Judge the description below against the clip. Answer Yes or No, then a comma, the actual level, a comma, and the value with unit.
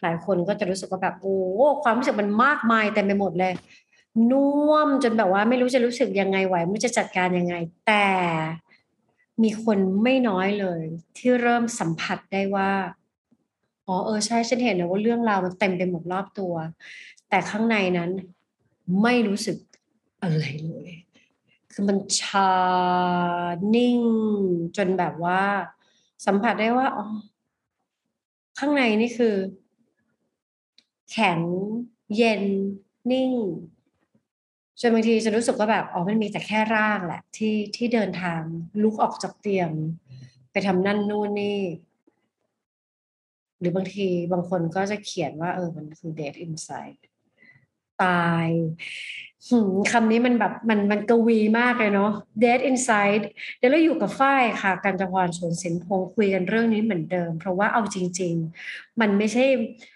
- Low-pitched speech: No, high, 200 Hz